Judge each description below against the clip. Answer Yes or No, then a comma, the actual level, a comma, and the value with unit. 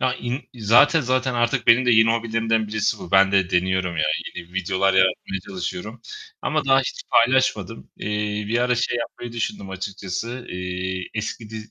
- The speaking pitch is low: Yes, low, 110 Hz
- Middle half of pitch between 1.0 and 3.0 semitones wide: No, average, 4.0 semitones